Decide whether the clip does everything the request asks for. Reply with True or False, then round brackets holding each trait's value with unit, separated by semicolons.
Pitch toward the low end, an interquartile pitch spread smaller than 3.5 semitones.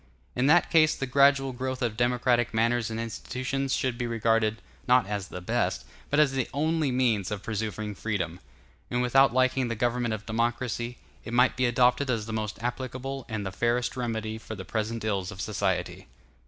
True (120 Hz; 2.8 semitones)